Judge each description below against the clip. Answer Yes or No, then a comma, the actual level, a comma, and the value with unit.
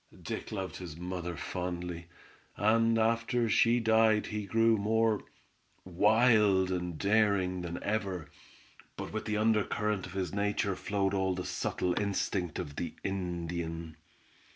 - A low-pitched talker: Yes, low, 100 Hz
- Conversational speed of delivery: No, slow, 130 wpm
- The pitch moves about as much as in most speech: Yes, average, 3.5 semitones